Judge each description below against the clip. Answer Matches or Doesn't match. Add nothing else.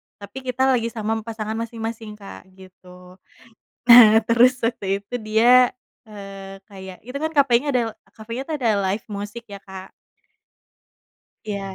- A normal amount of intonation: Matches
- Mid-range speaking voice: Doesn't match